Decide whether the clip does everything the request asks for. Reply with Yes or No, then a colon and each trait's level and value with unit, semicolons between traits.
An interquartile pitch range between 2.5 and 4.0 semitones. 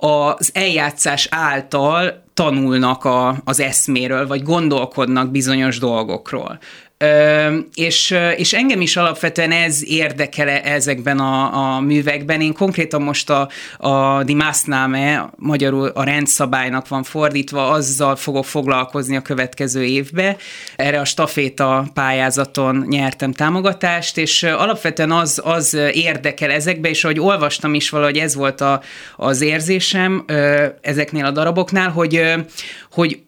Yes: average, 2.9 semitones